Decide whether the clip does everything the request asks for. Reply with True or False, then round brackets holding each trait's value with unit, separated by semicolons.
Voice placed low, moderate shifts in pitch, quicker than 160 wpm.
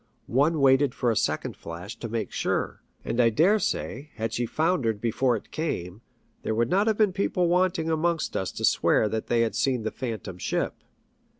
False (125 Hz; 6.4 semitones; 195 wpm)